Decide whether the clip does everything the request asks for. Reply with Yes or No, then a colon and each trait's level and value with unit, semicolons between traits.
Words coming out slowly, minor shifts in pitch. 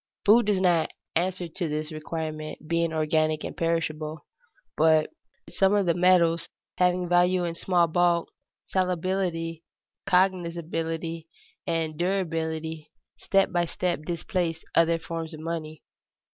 Yes: slow, 120 wpm; narrow, 2.0 semitones